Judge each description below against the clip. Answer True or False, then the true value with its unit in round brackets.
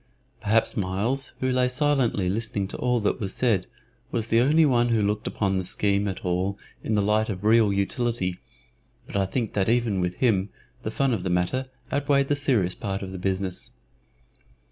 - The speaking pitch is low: True (105 Hz)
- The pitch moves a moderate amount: True (4.2 semitones)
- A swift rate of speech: False (190 wpm)